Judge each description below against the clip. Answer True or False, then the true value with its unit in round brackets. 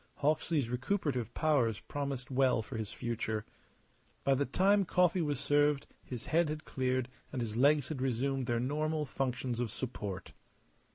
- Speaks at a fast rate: False (155 wpm)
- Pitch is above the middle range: False (135 Hz)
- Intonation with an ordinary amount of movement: True (3.5 semitones)